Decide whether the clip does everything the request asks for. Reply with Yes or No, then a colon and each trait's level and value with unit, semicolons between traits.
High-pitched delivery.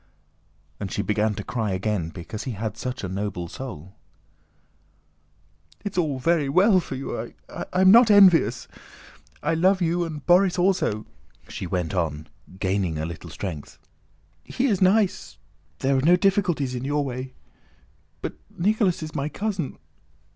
No: low, 135 Hz